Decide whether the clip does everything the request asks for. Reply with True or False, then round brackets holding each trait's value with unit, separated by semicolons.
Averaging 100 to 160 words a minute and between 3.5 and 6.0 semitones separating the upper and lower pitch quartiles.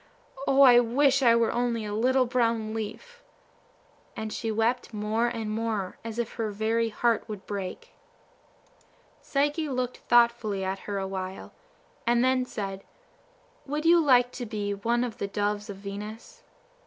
False (155 wpm; 3.0 semitones)